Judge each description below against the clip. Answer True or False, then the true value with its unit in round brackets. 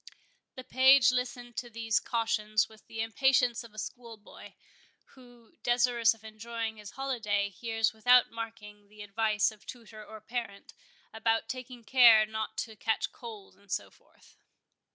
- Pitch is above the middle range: True (225 Hz)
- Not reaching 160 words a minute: True (150 wpm)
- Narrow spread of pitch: True (2.0 semitones)